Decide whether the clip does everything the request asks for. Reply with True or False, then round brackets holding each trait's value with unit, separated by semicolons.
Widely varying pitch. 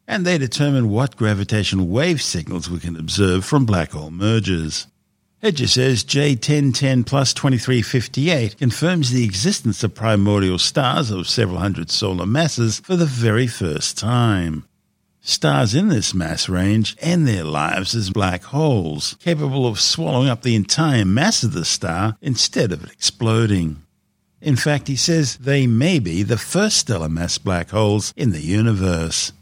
True (6.3 semitones)